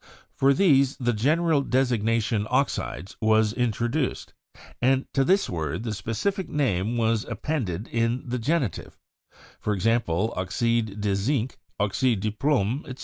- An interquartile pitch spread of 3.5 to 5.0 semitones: Yes, average, 4.2 semitones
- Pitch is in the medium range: No, low, 115 Hz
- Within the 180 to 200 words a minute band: No, average, 145 wpm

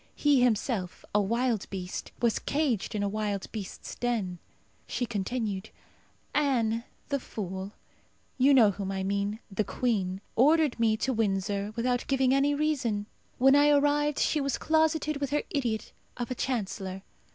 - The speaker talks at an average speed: Yes, average, 150 wpm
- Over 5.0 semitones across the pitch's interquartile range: Yes, wide, 5.4 semitones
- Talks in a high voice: Yes, high, 235 Hz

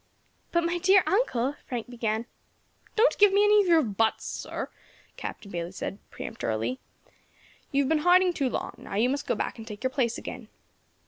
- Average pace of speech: Yes, average, 185 wpm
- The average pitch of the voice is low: No, very high, 260 Hz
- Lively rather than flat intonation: Yes, wide, 8.2 semitones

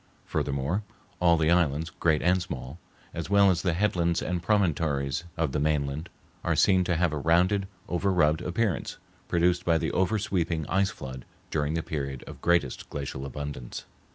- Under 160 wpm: No, average, 170 wpm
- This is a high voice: No, very low, 85 Hz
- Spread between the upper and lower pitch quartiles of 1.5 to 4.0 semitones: Yes, average, 3.6 semitones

